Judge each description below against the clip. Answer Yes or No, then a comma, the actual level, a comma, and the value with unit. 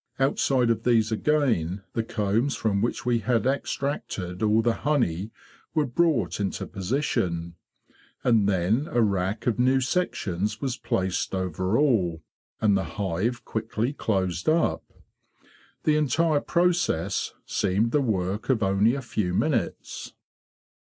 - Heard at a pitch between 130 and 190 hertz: No, low, 110 Hz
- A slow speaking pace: Yes, slow, 130 wpm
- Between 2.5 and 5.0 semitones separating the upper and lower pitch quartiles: No, wide, 5.5 semitones